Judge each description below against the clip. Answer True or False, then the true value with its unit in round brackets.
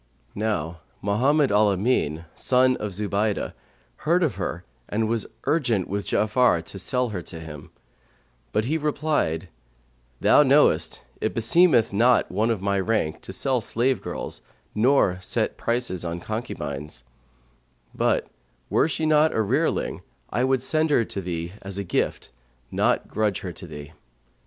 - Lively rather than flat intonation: True (5.8 semitones)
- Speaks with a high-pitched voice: False (110 Hz)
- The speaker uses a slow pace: False (150 wpm)